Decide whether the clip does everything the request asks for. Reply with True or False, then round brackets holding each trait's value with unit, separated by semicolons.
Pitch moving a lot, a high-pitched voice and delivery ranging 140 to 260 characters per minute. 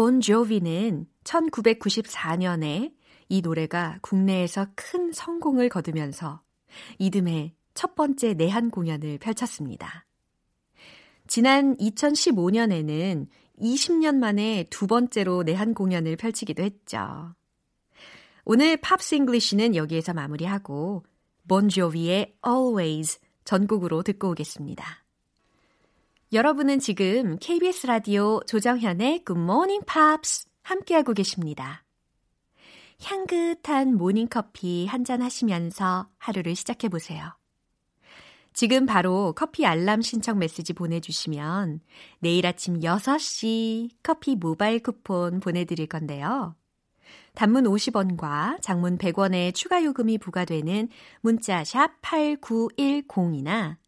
True (6.0 semitones; 205 Hz; 240 characters per minute)